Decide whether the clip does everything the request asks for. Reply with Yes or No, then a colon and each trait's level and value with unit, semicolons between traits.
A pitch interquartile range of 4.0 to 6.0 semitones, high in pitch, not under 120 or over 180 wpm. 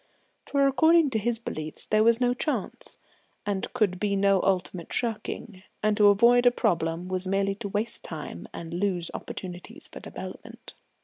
Yes: average, 4.3 semitones; high, 205 Hz; average, 165 wpm